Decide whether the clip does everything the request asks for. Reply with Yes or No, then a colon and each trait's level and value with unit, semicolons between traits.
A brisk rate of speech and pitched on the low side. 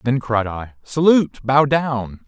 No: average, 160 wpm; low, 130 Hz